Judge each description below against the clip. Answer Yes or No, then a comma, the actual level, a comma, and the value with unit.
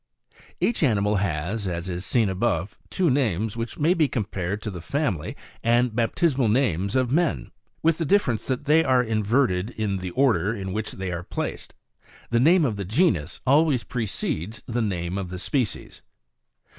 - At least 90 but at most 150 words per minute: No, average, 175 wpm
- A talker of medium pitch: No, low, 110 Hz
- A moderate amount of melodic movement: No, wide, 5.8 semitones